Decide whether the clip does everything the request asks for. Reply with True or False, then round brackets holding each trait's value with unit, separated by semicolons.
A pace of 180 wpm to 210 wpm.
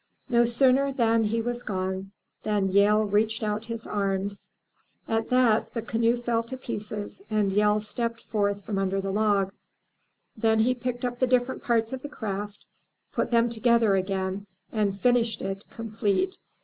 False (160 wpm)